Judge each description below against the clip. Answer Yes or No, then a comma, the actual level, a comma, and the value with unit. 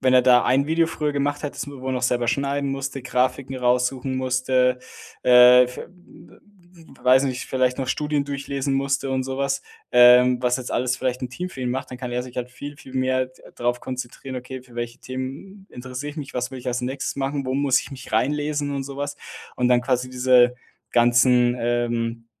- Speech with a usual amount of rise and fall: No, narrow, 1.8 semitones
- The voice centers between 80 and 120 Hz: No, low, 130 Hz